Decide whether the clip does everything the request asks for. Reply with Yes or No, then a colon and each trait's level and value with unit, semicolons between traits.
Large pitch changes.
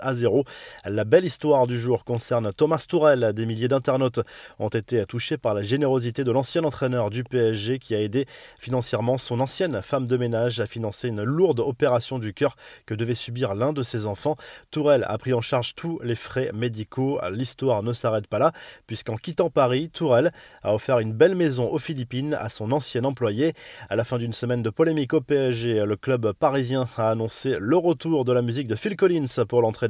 No: average, 3.3 semitones